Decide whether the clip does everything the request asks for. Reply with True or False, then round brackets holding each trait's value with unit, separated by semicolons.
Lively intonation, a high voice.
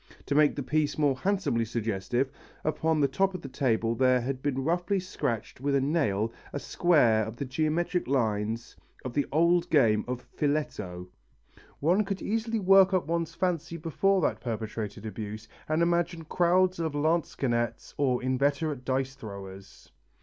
False (6.3 semitones; 140 Hz)